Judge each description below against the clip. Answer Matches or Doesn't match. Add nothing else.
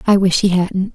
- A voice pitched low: Doesn't match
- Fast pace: Matches